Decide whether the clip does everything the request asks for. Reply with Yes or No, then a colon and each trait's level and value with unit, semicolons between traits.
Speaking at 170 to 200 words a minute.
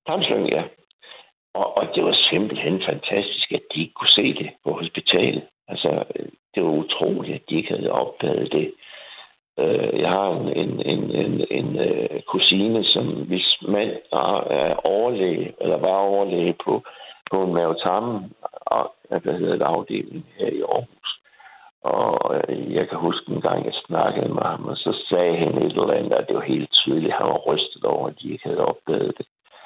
Yes: average, 180 wpm